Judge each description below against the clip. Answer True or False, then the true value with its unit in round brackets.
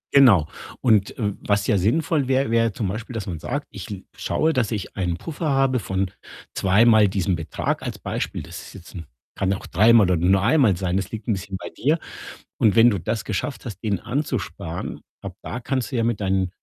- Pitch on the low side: True (105 Hz)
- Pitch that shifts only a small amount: False (4.5 semitones)